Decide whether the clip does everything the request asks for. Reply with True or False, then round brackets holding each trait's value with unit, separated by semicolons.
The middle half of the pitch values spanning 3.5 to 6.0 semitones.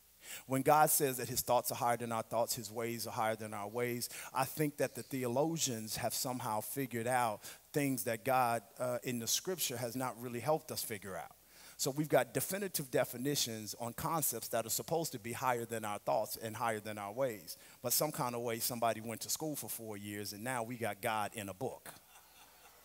False (2.9 semitones)